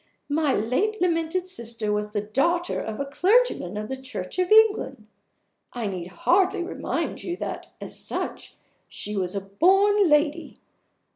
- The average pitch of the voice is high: Yes, very high, 295 Hz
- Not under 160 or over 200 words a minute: No, average, 150 wpm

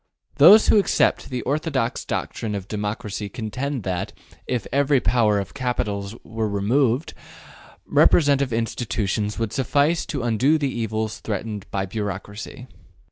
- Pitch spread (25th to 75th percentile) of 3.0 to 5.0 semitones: Yes, average, 4.7 semitones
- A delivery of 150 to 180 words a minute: No, slow, 135 wpm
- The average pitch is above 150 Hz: No, low, 115 Hz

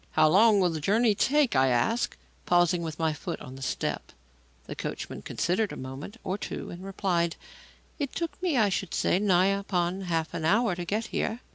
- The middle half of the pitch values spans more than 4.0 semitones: Yes, average, 4.5 semitones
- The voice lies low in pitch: No, medium, 185 Hz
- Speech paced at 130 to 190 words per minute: No, average, 200 wpm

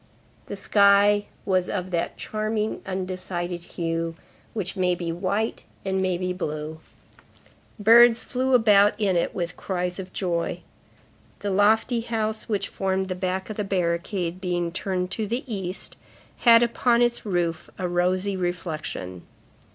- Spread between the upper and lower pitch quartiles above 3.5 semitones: No, average, 2.9 semitones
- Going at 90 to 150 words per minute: Yes, average, 145 wpm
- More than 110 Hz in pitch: Yes, high, 190 Hz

